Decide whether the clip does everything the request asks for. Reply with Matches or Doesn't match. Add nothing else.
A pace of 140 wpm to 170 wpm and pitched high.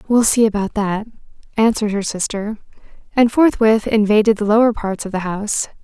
Matches